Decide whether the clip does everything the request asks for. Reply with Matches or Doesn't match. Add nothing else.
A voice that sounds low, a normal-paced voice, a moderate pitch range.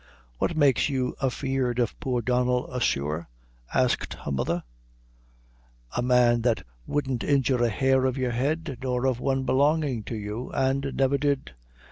Doesn't match